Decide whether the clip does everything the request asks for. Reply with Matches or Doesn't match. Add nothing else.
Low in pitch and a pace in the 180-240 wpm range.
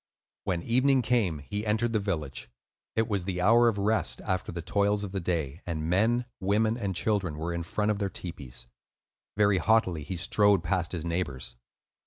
Matches